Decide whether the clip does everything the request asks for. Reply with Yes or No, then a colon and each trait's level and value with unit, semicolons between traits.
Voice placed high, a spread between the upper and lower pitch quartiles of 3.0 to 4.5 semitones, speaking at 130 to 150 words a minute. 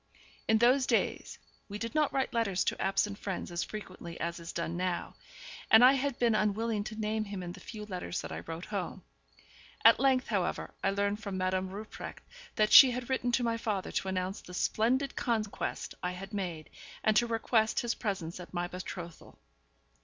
No: high, 205 Hz; average, 3.9 semitones; average, 190 wpm